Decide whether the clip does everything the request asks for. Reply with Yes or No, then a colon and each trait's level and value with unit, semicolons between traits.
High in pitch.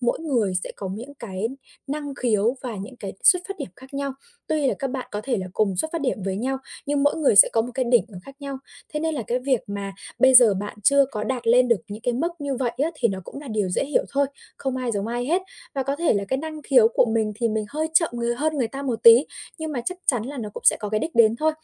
Yes: very high, 250 Hz